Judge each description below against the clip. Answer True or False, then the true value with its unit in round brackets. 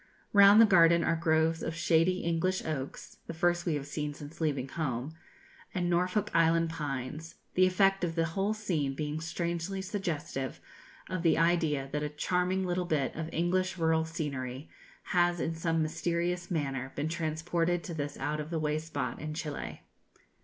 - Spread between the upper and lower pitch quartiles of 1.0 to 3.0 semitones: True (2.6 semitones)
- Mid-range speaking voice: True (165 Hz)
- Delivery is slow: False (170 wpm)